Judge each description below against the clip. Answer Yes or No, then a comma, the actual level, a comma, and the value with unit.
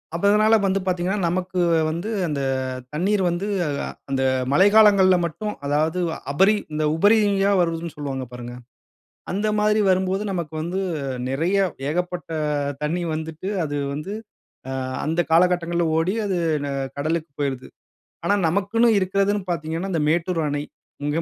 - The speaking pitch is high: No, medium, 175 Hz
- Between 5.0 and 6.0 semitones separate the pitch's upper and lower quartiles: No, average, 3.7 semitones